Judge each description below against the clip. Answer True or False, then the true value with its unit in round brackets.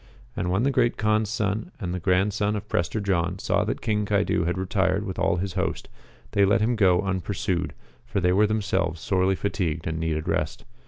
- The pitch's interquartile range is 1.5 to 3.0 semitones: True (2.7 semitones)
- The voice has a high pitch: False (95 Hz)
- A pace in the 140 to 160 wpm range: False (200 wpm)